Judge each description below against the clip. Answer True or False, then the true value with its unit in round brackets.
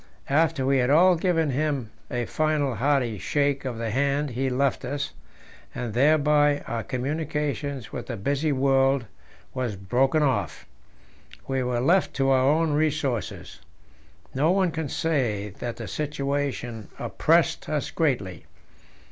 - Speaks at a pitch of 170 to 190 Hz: False (140 Hz)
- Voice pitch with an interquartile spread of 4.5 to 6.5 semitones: False (3.3 semitones)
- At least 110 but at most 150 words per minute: True (140 wpm)